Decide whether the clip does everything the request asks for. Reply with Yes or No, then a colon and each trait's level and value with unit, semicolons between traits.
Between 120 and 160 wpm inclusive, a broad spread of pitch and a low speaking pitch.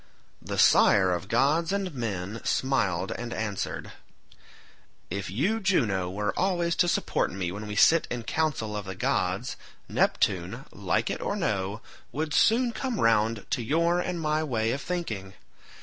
Yes: average, 155 wpm; wide, 8.7 semitones; low, 115 Hz